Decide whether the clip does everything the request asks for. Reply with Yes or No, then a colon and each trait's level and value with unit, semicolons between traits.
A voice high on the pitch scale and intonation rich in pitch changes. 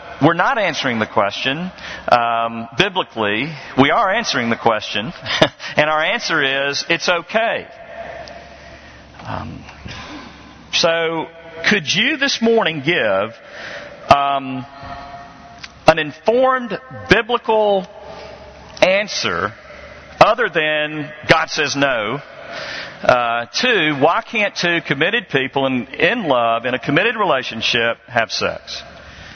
No: medium, 155 Hz; wide, 7.8 semitones